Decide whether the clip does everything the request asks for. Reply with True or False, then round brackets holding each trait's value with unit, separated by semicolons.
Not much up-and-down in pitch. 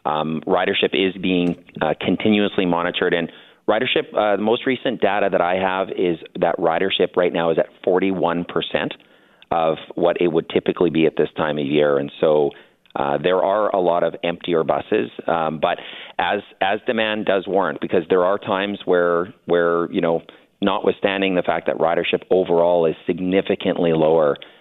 True (2.0 semitones)